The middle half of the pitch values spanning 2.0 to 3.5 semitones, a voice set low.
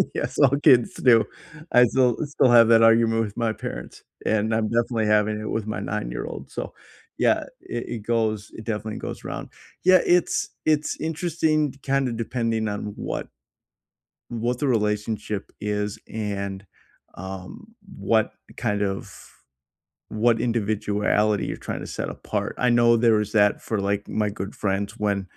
Yes: narrow, 2.4 semitones; low, 110 Hz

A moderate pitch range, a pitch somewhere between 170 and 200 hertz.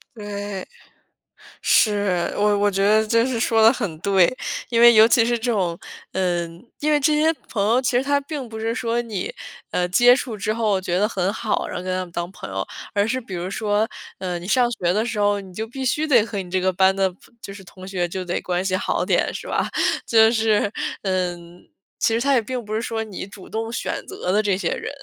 No: average, 3.7 semitones; high, 210 Hz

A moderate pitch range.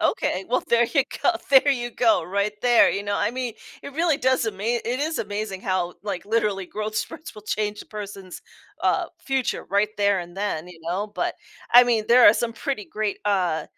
Yes: average, 3.4 semitones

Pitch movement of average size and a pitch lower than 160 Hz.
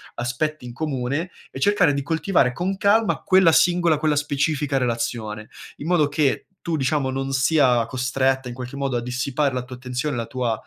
Yes: average, 3.7 semitones; low, 135 Hz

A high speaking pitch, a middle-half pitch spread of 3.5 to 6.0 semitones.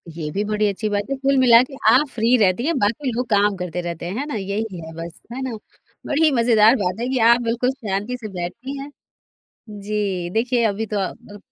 Yes: high, 215 Hz; average, 4.2 semitones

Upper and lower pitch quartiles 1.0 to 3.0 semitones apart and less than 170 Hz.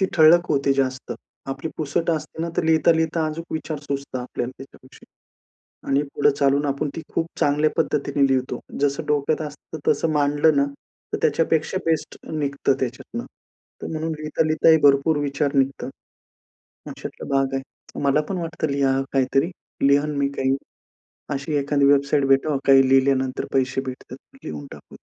Yes: narrow, 2.4 semitones; medium, 140 Hz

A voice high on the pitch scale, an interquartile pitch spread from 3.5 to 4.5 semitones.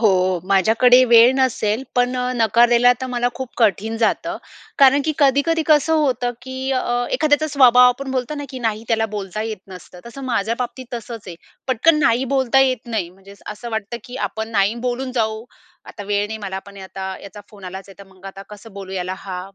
Yes: high, 230 Hz; average, 4.2 semitones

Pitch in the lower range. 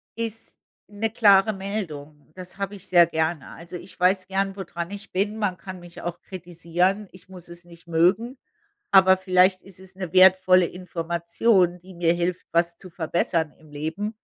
No: medium, 185 Hz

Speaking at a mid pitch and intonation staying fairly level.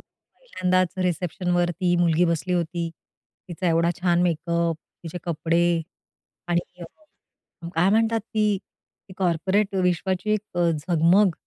Yes: medium, 175 Hz; narrow, 1.9 semitones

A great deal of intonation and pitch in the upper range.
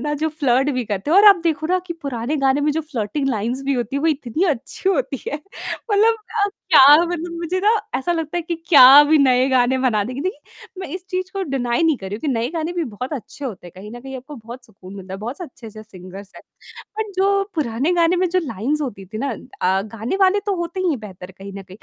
Yes: wide, 6.6 semitones; very high, 275 Hz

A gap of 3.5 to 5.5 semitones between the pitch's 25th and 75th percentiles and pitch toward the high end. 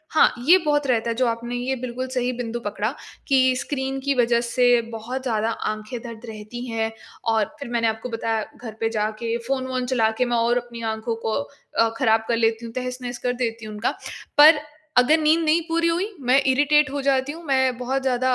No: average, 2.7 semitones; high, 245 Hz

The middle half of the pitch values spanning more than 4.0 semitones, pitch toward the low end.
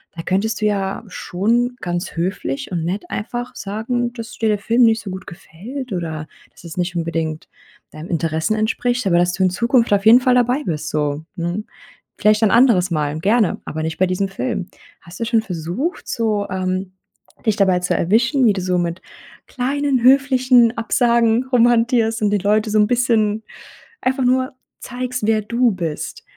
No: average, 5.1 semitones; high, 215 Hz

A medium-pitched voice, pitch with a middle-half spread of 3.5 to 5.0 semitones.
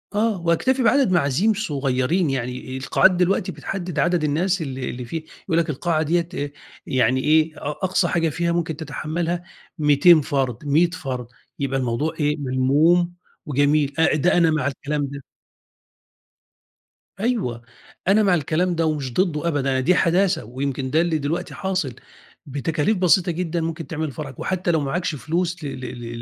Yes: medium, 155 Hz; average, 4.1 semitones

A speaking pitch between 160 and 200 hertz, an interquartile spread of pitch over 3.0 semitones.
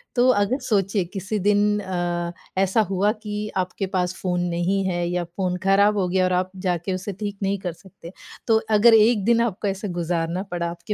No: high, 190 Hz; narrow, 2.6 semitones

